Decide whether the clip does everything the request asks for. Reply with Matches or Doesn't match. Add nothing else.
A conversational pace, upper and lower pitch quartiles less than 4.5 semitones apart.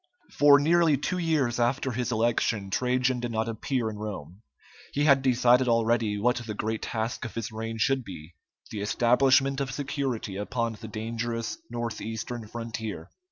Matches